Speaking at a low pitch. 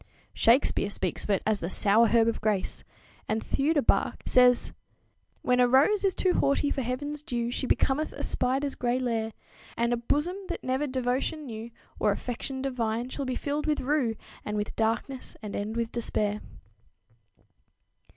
No: high, 245 Hz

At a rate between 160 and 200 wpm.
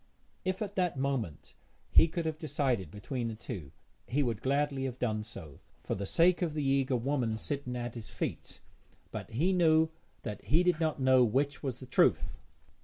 Yes: average, 185 wpm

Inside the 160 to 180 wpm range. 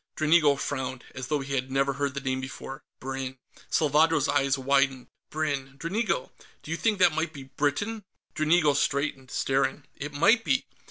Yes: average, 165 wpm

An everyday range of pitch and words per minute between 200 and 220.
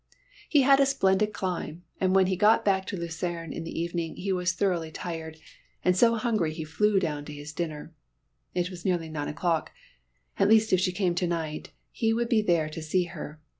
Yes: average, 3.4 semitones; fast, 205 wpm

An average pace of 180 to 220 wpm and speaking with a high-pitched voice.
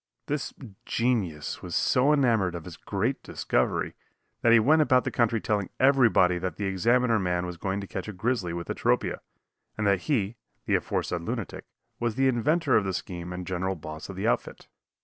No: average, 190 wpm; low, 105 Hz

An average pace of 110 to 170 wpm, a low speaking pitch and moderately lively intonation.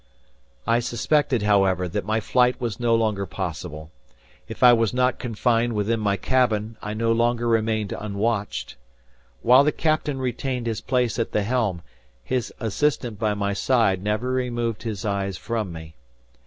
Yes: average, 155 wpm; low, 115 Hz; average, 3.1 semitones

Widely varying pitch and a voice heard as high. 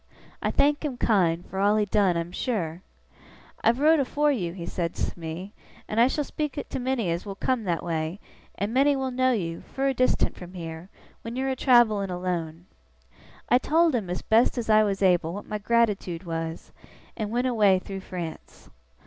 Yes: wide, 6.3 semitones; high, 205 Hz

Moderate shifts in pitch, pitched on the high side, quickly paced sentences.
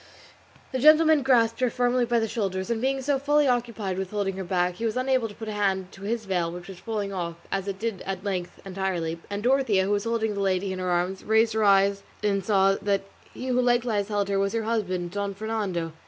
Yes: average, 3.4 semitones; high, 205 Hz; fast, 230 wpm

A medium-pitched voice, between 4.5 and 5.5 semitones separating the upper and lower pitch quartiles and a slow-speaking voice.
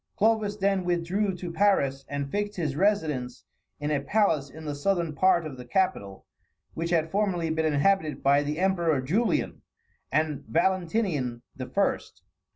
No: medium, 165 Hz; average, 5.1 semitones; average, 155 wpm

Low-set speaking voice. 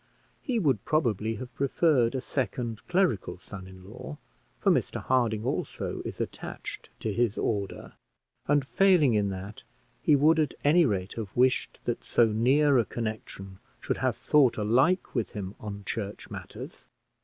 Yes: low, 115 Hz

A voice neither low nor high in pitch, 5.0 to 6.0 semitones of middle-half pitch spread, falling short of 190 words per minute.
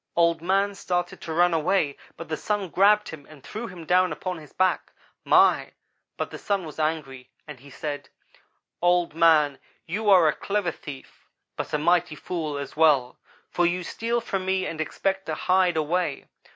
No: medium, 170 Hz; average, 3.4 semitones; average, 180 wpm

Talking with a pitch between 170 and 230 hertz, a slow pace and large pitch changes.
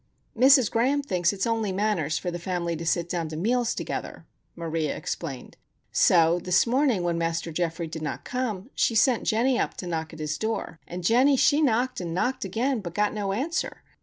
No: high, 190 Hz; average, 195 wpm; wide, 6.2 semitones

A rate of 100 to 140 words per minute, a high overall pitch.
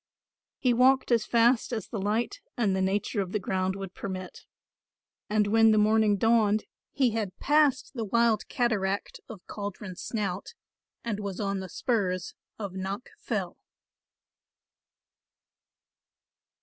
Yes: slow, 135 wpm; high, 210 Hz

